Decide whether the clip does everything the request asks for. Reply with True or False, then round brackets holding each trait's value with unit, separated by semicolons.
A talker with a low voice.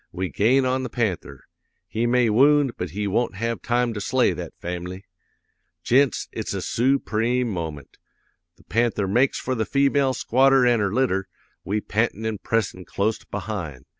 True (110 Hz)